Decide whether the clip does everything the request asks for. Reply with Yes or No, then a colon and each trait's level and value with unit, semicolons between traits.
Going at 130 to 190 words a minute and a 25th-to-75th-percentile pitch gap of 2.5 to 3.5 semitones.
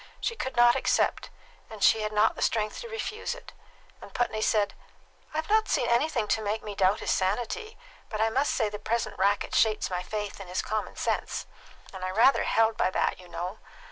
No: fast, 205 wpm; average, 3.0 semitones